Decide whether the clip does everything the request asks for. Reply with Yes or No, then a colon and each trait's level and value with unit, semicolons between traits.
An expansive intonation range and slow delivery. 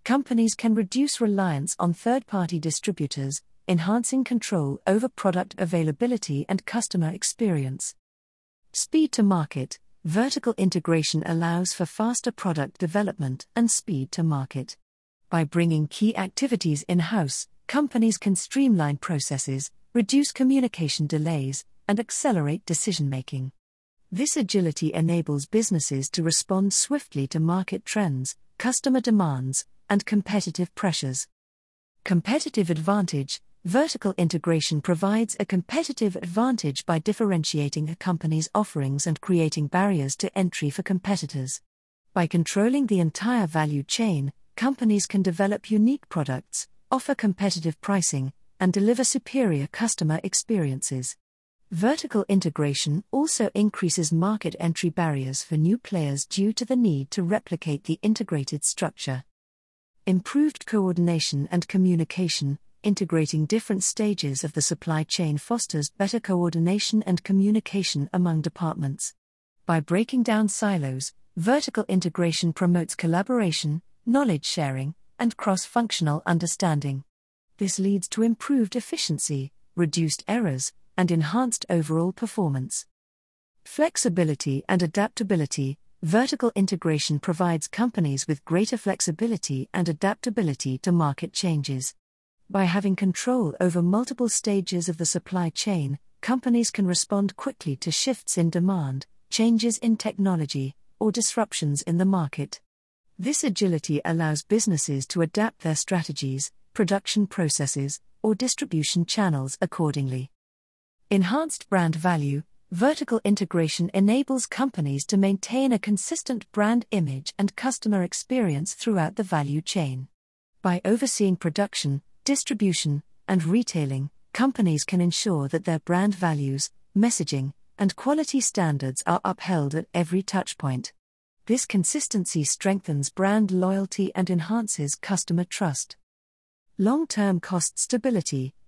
Yes: wide, 5.7 semitones; slow, 120 wpm